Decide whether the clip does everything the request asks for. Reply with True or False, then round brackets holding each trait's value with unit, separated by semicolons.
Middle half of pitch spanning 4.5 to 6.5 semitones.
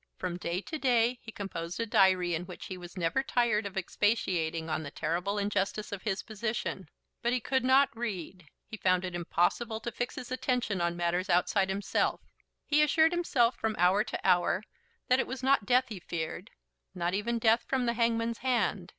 True (5.0 semitones)